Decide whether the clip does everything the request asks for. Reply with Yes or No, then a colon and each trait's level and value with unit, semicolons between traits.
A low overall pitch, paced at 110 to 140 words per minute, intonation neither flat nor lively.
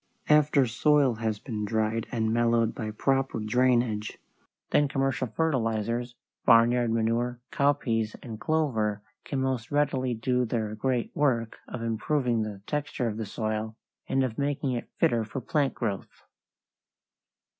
Yes: low, 120 Hz; slow, 135 wpm; average, 3.3 semitones